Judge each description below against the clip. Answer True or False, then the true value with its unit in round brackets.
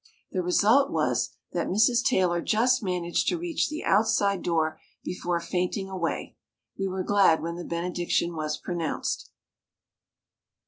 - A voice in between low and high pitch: True (180 Hz)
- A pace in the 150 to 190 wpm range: False (135 wpm)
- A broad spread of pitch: False (3.6 semitones)